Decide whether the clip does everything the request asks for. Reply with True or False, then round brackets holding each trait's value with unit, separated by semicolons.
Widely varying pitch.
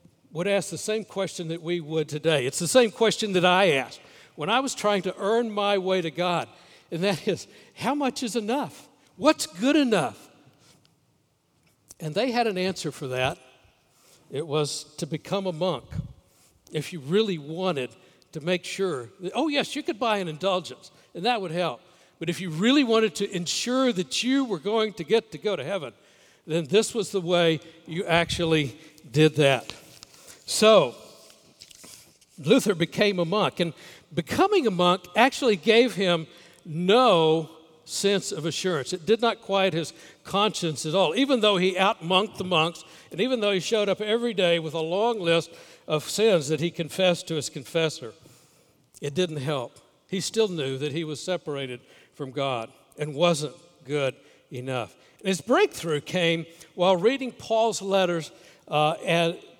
False (4.8 semitones)